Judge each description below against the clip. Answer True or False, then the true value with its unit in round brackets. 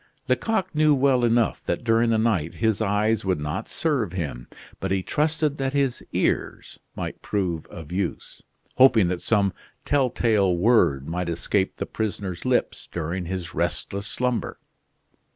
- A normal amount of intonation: False (5.9 semitones)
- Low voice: True (105 Hz)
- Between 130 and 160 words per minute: True (150 wpm)